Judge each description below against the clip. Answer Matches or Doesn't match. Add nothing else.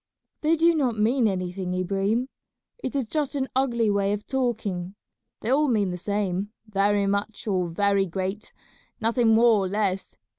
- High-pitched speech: Matches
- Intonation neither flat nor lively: Matches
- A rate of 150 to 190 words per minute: Matches